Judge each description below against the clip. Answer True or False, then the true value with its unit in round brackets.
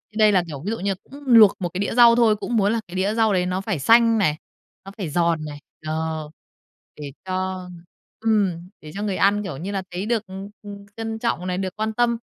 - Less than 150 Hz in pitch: False (195 Hz)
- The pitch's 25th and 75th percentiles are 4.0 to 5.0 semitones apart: False (3.6 semitones)